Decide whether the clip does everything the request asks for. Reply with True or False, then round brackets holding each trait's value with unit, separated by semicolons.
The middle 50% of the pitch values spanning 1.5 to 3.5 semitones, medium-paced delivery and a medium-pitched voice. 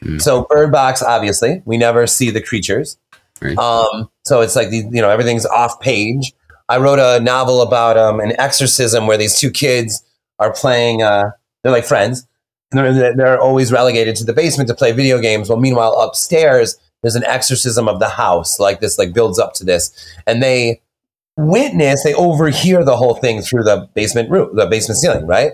False (2.7 semitones; 190 wpm; 120 Hz)